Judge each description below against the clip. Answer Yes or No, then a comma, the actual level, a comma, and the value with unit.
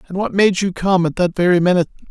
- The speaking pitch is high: No, medium, 180 Hz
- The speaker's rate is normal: No, fast, 255 wpm